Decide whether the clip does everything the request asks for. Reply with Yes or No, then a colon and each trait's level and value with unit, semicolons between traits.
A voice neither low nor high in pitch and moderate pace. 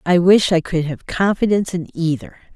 Yes: medium, 175 Hz; average, 190 wpm